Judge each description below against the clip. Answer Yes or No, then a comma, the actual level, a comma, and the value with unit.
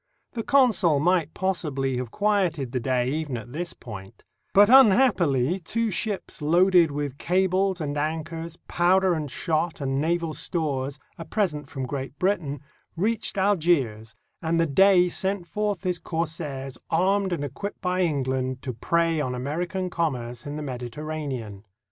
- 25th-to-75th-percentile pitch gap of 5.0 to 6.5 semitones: Yes, average, 5.3 semitones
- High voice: No, medium, 160 Hz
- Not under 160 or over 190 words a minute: No, average, 150 wpm